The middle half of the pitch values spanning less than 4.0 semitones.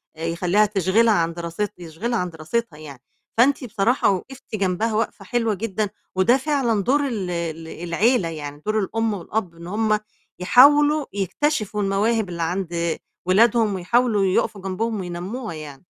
No: average, 4.9 semitones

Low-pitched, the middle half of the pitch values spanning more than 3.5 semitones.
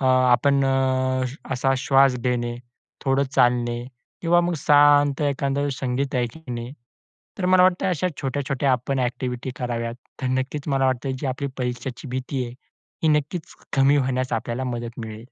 No: low, 130 Hz; narrow, 2.4 semitones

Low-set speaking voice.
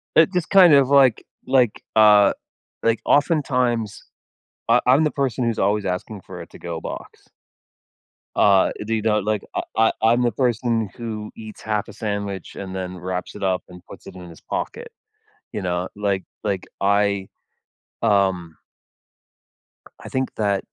Yes: low, 105 Hz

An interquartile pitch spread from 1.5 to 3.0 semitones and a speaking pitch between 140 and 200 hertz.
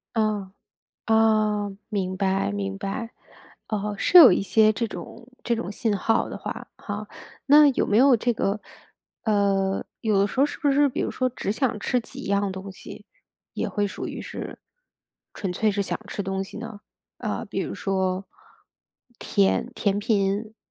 No: average, 2.7 semitones; high, 210 Hz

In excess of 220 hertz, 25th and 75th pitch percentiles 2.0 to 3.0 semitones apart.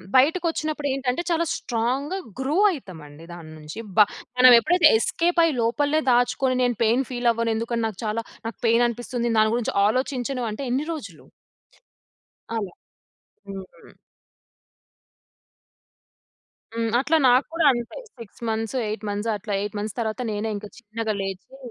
No: high, 235 Hz; average, 3.7 semitones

